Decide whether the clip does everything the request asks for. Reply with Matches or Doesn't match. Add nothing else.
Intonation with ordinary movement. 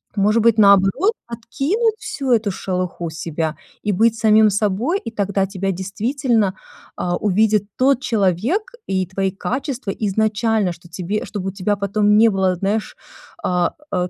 Matches